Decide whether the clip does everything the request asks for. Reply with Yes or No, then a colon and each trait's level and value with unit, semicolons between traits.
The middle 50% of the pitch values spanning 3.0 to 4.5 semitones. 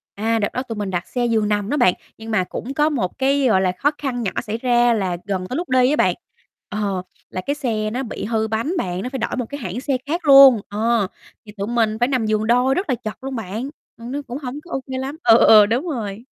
Yes: average, 4.0 semitones